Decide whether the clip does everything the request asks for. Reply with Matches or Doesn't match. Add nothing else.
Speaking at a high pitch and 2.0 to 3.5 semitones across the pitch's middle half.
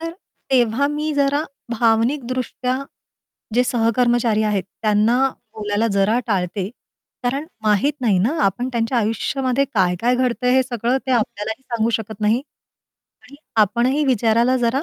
Matches